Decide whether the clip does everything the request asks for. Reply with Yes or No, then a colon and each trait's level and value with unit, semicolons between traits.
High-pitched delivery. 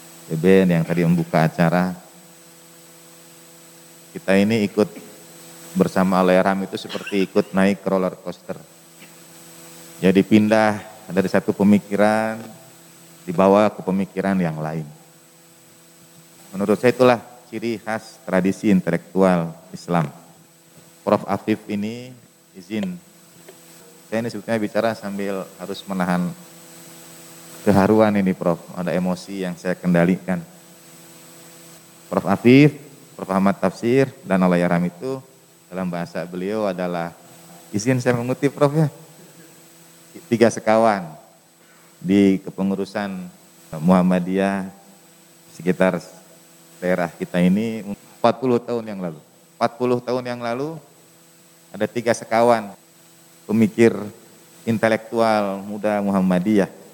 No: very low, 95 Hz